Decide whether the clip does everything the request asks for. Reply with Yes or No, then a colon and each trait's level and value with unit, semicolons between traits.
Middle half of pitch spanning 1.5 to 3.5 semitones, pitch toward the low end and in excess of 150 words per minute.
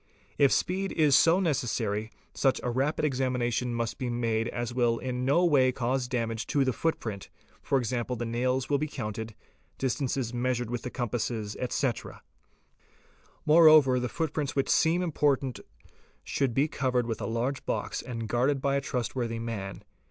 Yes: average, 2.9 semitones; low, 125 Hz; average, 160 wpm